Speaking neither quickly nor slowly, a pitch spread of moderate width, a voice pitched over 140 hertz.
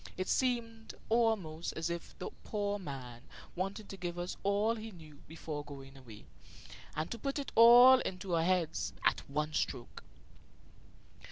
No: average, 155 wpm; wide, 6.2 semitones; medium, 185 Hz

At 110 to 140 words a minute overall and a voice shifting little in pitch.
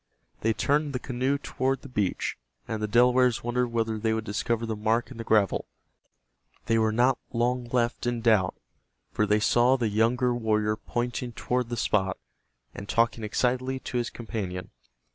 No: average, 170 wpm; narrow, 2.2 semitones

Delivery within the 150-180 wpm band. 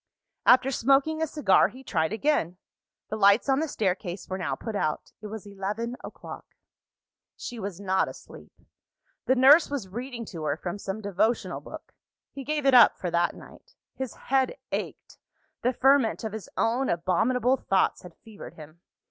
Yes: average, 170 wpm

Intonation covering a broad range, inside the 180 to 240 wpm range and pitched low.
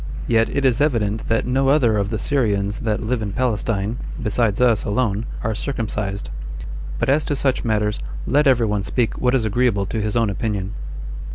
No: average, 3.2 semitones; average, 185 wpm; low, 115 Hz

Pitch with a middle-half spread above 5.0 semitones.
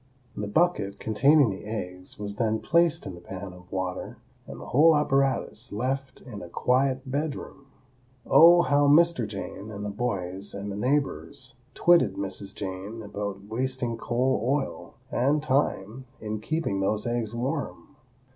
Yes: wide, 5.5 semitones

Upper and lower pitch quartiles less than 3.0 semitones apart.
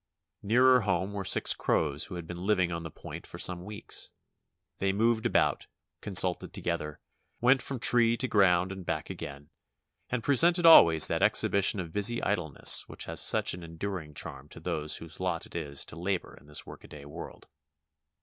No: average, 4.6 semitones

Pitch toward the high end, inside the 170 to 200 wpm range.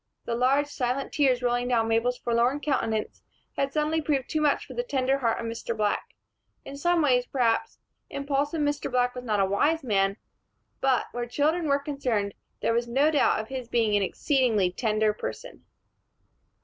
Yes: very high, 250 Hz; average, 175 wpm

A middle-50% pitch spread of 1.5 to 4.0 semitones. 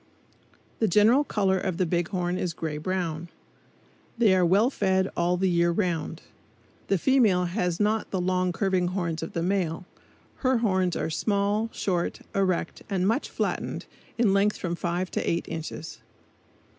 Yes: average, 2.7 semitones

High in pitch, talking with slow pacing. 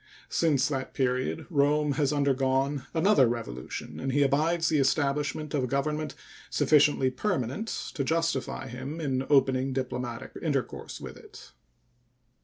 No: medium, 140 Hz; slow, 130 wpm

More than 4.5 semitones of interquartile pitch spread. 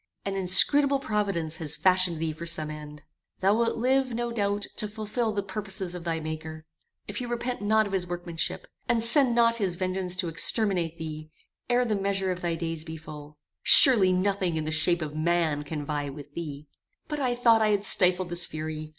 Yes: average, 4.9 semitones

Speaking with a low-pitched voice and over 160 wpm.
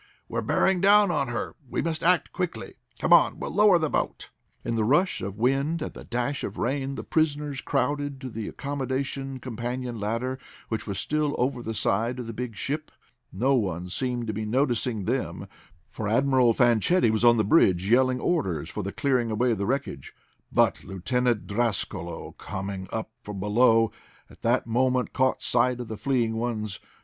Yes: low, 125 Hz; average, 180 wpm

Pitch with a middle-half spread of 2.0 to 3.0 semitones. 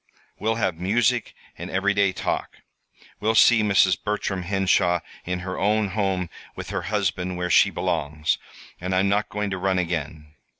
Yes: narrow, 2.6 semitones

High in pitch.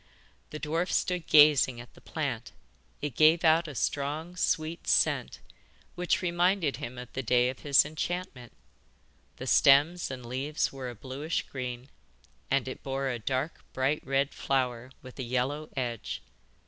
No: medium, 140 Hz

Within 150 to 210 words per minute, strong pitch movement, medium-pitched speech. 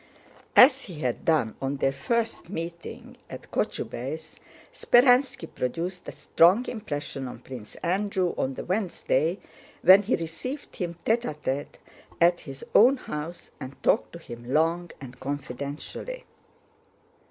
No: slow, 135 wpm; wide, 6.4 semitones; medium, 165 Hz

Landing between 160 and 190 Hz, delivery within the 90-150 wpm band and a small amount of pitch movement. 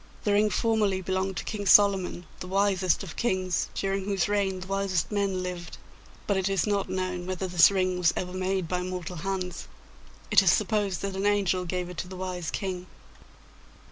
No: medium, 185 Hz; average, 190 wpm; narrow, 1.5 semitones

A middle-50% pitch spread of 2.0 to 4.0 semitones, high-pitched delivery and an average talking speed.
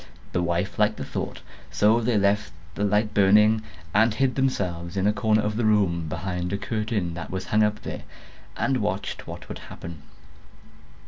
No: average, 3.2 semitones; low, 105 Hz; average, 180 wpm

